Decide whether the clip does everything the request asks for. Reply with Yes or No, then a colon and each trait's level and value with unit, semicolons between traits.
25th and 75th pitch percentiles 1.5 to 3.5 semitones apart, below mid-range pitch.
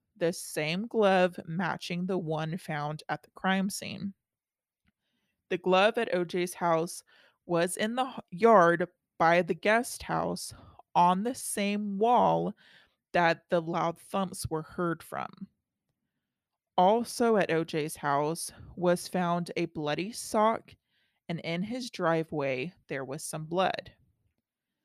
No: average, 3.1 semitones; medium, 180 Hz